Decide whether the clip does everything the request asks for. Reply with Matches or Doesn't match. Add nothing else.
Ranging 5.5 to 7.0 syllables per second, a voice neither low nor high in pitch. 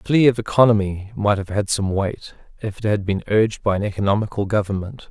Doesn't match